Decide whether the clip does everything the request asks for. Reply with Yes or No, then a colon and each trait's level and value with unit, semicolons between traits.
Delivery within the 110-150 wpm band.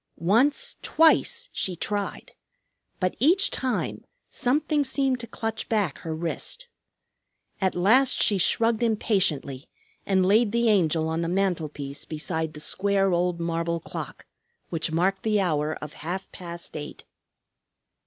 Yes: slow, 135 wpm